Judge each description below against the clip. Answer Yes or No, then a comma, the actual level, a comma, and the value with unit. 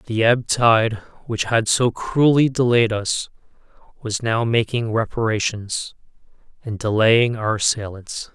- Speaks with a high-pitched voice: No, low, 115 Hz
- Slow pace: Yes, slow, 120 wpm